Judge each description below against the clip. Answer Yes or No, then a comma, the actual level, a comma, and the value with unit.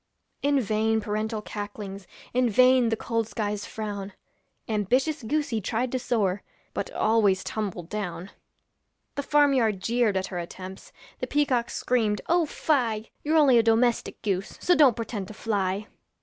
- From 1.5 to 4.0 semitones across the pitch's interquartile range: Yes, average, 3.6 semitones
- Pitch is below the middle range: No, high, 220 Hz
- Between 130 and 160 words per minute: Yes, average, 150 wpm